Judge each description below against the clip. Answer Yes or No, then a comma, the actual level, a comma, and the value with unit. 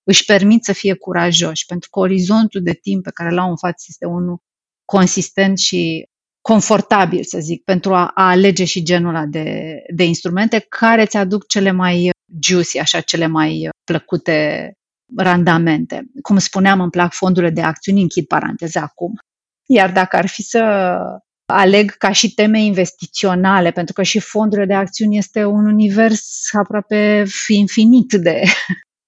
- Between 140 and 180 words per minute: Yes, average, 155 wpm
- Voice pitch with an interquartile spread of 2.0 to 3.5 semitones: Yes, average, 2.9 semitones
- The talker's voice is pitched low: No, high, 190 Hz